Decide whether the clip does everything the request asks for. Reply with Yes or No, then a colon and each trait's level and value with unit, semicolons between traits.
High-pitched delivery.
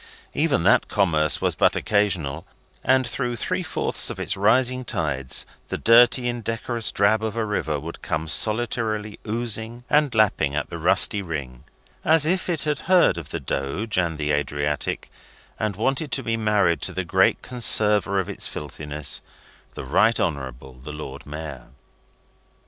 No: low, 105 Hz